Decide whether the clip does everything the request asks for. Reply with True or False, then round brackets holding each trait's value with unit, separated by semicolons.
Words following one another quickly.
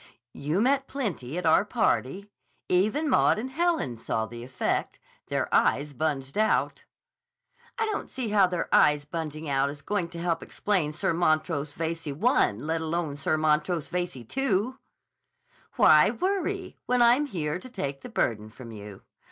False (160 wpm)